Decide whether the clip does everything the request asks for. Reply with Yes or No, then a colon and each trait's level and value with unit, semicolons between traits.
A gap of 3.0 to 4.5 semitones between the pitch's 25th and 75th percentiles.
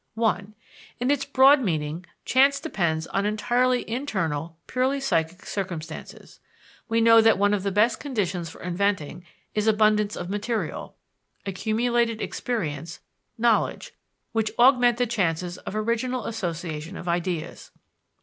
No: wide, 5.4 semitones